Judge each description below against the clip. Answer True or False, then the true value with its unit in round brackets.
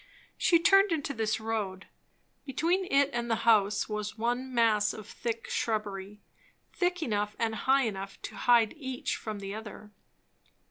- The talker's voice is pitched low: False (225 Hz)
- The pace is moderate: True (150 wpm)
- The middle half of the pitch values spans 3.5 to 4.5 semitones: True (4.0 semitones)